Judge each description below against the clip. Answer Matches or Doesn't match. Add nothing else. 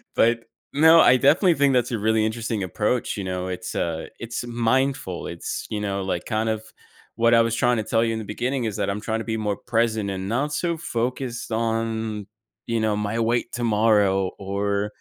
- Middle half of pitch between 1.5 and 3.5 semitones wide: Matches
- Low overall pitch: Matches